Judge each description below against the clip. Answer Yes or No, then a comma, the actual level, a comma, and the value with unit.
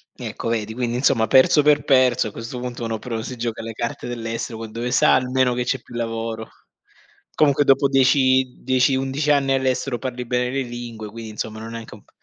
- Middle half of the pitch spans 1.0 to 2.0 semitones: No, narrow, 2.4 semitones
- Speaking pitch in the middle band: No, low, 125 Hz